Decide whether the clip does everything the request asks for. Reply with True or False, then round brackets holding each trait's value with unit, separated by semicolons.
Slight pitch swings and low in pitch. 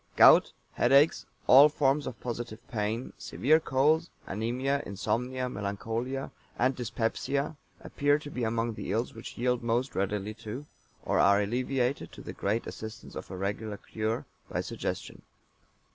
False (3.7 semitones; 120 Hz)